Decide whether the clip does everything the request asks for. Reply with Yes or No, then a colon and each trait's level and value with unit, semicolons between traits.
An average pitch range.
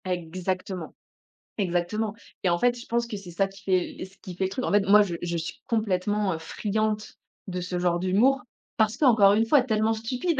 Yes: average, 3.4 semitones